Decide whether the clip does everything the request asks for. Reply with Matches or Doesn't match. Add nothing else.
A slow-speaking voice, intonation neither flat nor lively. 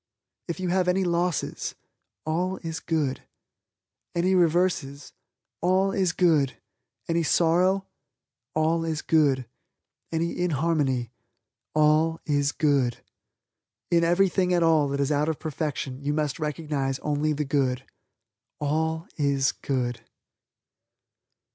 Matches